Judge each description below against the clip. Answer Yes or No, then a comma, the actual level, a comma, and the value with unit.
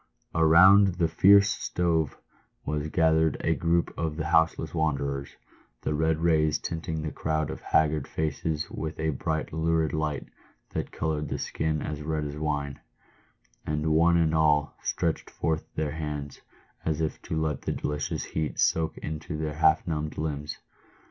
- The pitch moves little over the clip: Yes, narrow, 1.1 semitones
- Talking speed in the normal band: Yes, average, 155 wpm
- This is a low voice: Yes, very low, 80 Hz